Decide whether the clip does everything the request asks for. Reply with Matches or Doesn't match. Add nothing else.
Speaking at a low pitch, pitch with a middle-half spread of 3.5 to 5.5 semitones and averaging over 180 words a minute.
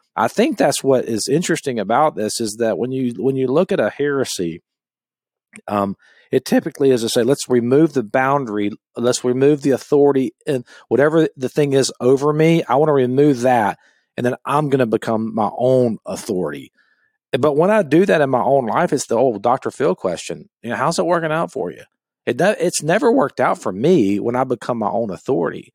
Matches